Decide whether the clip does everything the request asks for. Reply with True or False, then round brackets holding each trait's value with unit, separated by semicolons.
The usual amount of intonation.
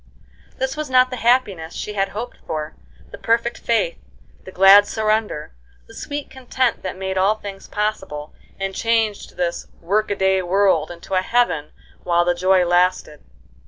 True (4.3 semitones)